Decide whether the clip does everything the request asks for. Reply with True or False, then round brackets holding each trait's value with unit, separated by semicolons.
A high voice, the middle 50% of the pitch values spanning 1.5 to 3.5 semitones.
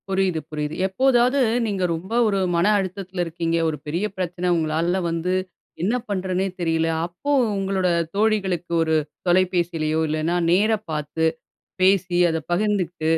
False (180 Hz; 2.9 semitones)